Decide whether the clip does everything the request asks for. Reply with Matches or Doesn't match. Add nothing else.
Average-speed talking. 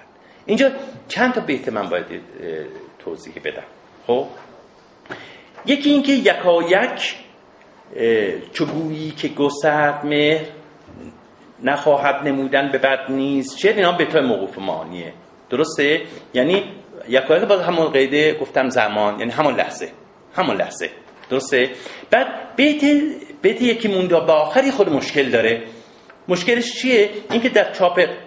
Matches